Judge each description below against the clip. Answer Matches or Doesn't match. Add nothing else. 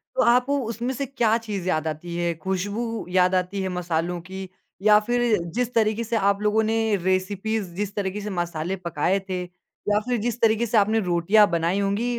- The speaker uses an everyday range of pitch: Matches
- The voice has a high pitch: Matches